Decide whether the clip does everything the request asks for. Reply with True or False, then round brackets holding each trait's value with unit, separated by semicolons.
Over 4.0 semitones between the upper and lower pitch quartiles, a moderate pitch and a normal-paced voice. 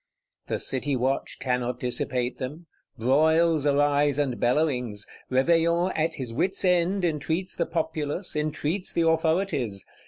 False (4.5 semitones; 150 Hz; 125 wpm)